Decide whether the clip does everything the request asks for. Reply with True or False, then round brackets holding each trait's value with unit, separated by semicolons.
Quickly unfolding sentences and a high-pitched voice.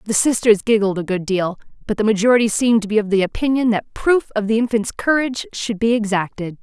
True (215 wpm; 220 Hz)